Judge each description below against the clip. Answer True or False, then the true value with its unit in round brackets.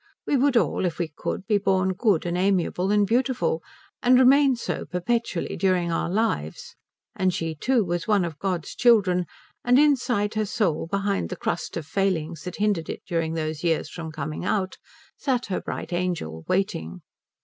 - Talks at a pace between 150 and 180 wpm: True (175 wpm)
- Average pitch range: True (4.8 semitones)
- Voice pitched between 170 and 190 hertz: True (185 Hz)